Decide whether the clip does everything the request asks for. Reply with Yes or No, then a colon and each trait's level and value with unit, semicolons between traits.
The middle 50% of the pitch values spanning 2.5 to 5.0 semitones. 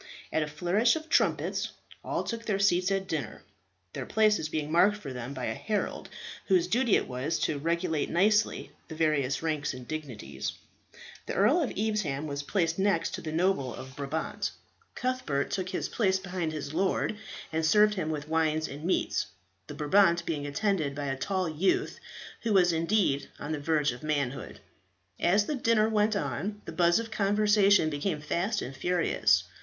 No: wide, 5.5 semitones